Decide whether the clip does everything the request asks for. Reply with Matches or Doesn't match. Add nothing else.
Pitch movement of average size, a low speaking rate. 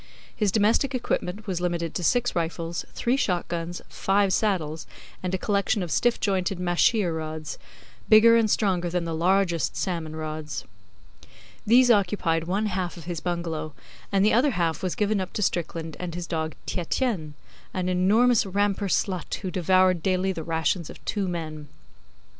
Doesn't match